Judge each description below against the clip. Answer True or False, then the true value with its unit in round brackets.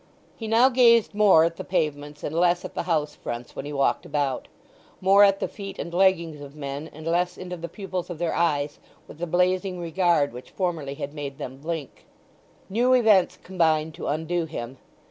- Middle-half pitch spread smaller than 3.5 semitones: False (4.0 semitones)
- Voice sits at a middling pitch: True (170 Hz)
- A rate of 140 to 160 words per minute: False (195 wpm)